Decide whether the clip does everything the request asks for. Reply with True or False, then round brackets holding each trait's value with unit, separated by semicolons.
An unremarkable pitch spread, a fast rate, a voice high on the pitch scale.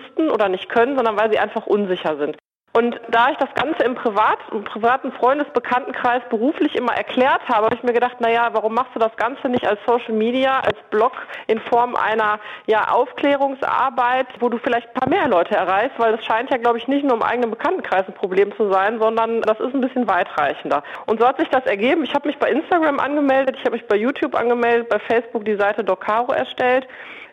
True (3.1 semitones; 215 wpm; 240 Hz)